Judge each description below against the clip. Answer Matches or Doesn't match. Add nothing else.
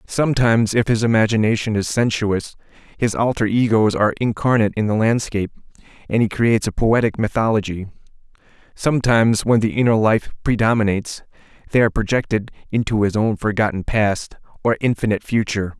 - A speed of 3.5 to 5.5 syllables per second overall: Doesn't match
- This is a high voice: Doesn't match